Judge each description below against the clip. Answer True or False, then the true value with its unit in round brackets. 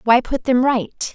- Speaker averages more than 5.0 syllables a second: False (3.8 syllables/s)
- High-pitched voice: True (245 Hz)